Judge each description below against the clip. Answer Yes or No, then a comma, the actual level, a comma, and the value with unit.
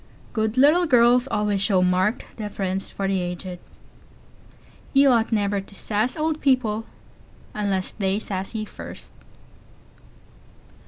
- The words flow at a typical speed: No, slow, 120 wpm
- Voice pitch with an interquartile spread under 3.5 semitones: No, average, 4.0 semitones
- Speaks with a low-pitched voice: No, high, 210 Hz